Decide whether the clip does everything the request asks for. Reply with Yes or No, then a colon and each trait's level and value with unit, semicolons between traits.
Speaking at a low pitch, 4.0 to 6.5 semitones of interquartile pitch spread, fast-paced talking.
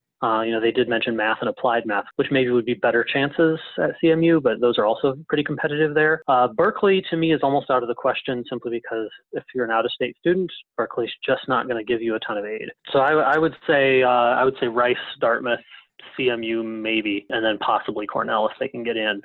Yes: low, 125 Hz; average, 4.5 semitones; fast, 235 wpm